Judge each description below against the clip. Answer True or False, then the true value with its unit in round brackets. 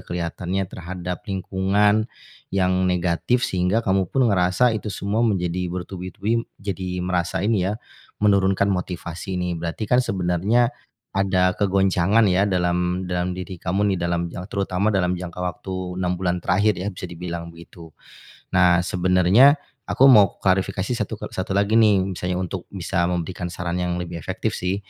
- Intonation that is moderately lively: False (1.9 semitones)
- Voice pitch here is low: True (90 Hz)